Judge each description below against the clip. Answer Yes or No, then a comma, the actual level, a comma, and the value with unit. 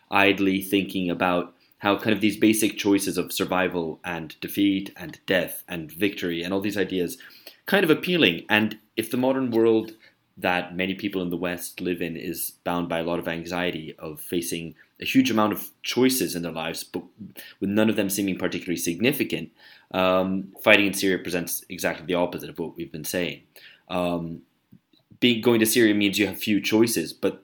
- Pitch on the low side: Yes, very low, 95 Hz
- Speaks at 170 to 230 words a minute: Yes, average, 190 wpm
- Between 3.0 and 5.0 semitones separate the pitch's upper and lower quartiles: Yes, average, 3.4 semitones